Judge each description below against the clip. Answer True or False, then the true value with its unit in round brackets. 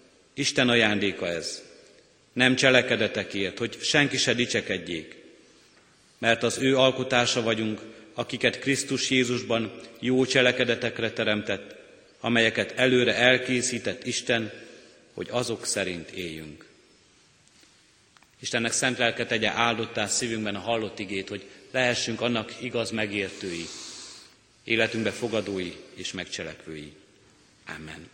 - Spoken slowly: True (100 wpm)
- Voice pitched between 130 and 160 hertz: False (115 Hz)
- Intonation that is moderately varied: True (3.0 semitones)